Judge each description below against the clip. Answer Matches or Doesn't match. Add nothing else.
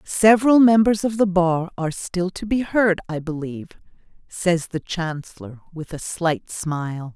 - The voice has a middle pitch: Matches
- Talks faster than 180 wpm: Doesn't match